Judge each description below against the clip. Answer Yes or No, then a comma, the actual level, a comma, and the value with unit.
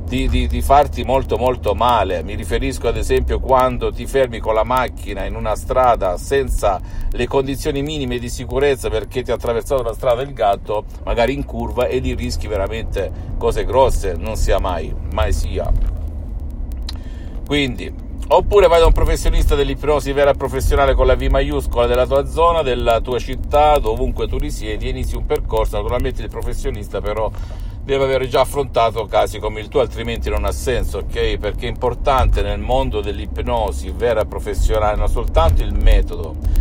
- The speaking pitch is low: Yes, low, 105 Hz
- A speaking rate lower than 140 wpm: No, fast, 170 wpm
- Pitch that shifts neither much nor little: No, wide, 8.9 semitones